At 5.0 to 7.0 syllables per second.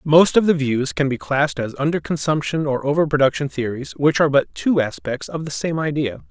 Yes: 5.6 syllables/s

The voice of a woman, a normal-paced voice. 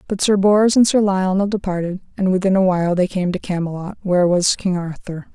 No: female; fast, 215 wpm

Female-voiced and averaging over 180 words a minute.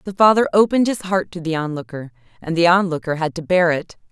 Yes: female; fast, 205 wpm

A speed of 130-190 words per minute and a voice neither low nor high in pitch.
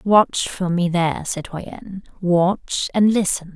Yes: slow, 135 wpm; medium, 180 Hz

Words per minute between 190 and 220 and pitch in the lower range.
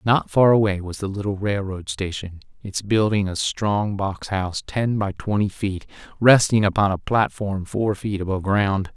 No: average, 175 wpm; low, 100 Hz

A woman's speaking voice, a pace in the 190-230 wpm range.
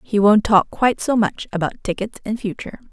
Yes: female; fast, 205 wpm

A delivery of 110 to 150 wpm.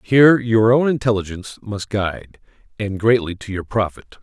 Yes: average, 140 wpm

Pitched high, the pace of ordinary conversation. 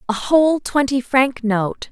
Yes: very high, 255 Hz; average, 155 wpm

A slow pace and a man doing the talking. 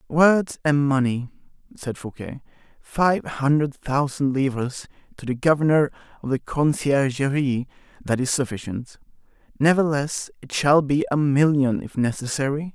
Yes: slow, 120 wpm; male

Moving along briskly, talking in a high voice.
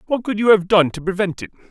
Yes: fast, 280 wpm; high, 195 Hz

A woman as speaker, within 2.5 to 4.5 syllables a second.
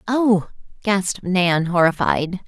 Yes: female; 3.6 syllables/s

